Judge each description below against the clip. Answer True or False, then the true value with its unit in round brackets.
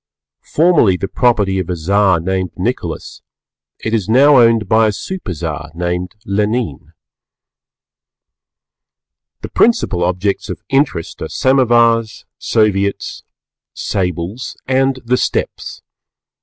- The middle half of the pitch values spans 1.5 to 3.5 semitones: False (5.2 semitones)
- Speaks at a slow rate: True (105 wpm)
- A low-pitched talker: True (105 Hz)